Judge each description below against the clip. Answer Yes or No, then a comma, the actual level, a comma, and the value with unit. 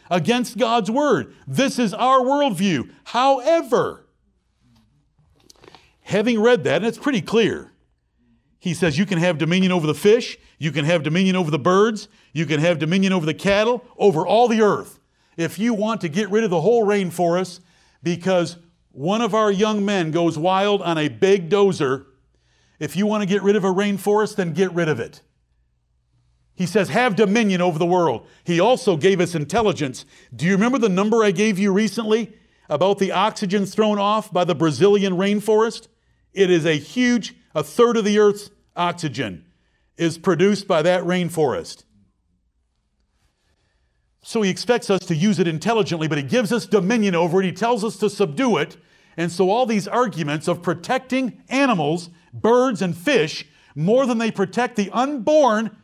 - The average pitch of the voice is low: No, high, 195 Hz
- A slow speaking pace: No, average, 175 wpm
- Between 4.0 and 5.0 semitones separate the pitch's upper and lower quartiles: Yes, average, 4.7 semitones